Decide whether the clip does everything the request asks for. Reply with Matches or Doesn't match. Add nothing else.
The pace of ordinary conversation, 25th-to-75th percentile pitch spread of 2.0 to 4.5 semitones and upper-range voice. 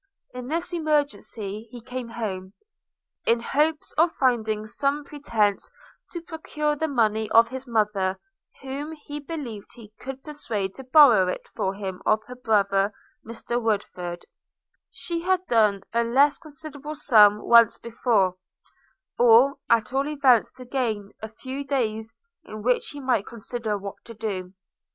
Doesn't match